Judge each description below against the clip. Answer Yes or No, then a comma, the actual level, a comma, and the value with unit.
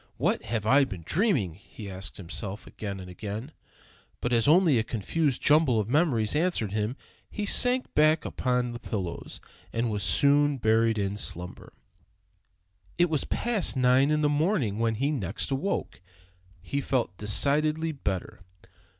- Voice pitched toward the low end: Yes, low, 125 Hz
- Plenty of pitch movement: Yes, wide, 6.4 semitones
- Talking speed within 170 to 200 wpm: No, average, 155 wpm